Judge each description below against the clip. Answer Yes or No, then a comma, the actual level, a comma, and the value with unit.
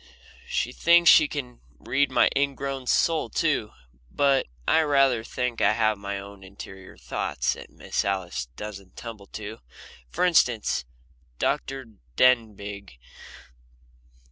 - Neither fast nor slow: No, slow, 120 wpm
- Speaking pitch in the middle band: No, low, 115 Hz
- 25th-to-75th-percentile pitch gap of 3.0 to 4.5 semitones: No, wide, 5.4 semitones